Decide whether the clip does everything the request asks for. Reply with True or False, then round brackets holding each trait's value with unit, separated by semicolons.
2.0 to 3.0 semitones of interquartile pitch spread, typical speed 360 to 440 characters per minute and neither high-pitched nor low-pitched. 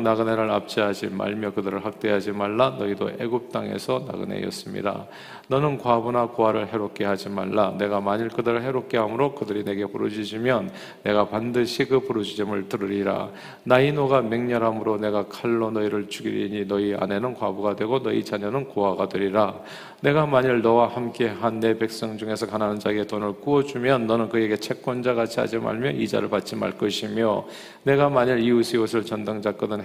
False (2.7 semitones; 390 characters per minute; 110 Hz)